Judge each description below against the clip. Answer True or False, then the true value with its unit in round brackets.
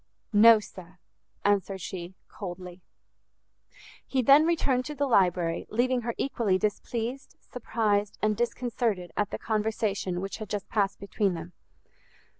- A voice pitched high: True (210 Hz)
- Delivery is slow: True (130 wpm)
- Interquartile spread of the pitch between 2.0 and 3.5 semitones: False (4.0 semitones)